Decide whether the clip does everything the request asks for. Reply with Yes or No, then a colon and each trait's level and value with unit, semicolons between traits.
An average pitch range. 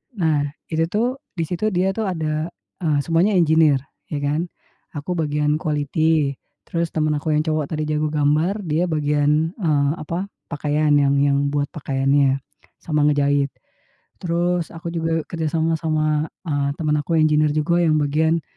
No: narrow, 2.1 semitones